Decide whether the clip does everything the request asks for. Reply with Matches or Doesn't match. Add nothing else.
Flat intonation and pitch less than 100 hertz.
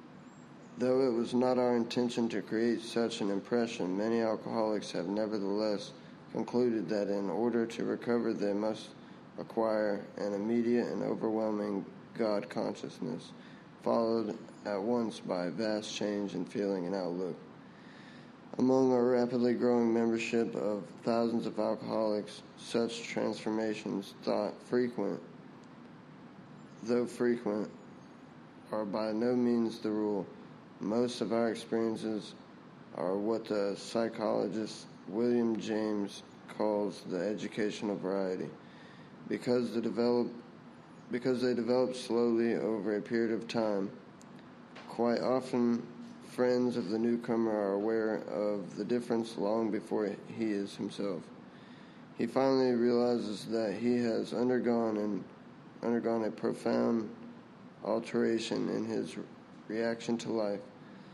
Doesn't match